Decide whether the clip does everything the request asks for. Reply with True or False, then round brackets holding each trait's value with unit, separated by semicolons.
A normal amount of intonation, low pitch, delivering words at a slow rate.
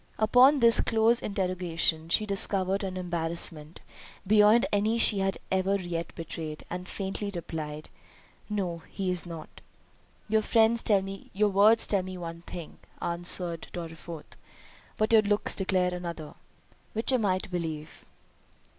False (3.6 semitones; 185 Hz; 125 wpm)